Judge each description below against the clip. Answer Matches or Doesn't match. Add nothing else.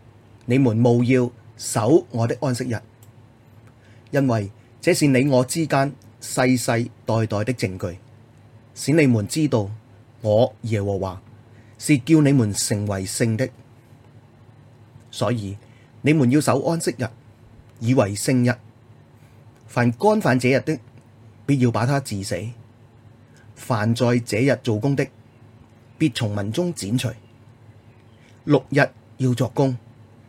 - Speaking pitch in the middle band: Doesn't match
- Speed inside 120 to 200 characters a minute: Matches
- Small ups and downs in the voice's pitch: Matches